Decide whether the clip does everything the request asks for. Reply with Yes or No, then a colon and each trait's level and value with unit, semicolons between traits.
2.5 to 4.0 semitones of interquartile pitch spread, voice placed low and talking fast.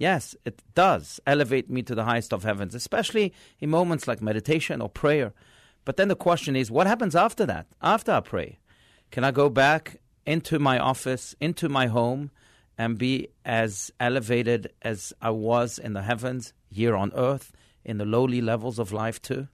No: average, 3.5 semitones; low, 125 Hz; average, 180 wpm